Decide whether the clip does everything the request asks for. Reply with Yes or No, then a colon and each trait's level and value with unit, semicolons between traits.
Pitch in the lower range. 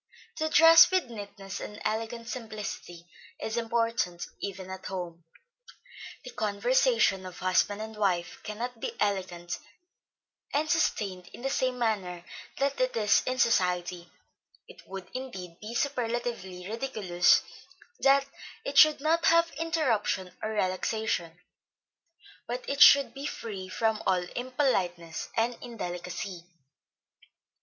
No: high, 215 Hz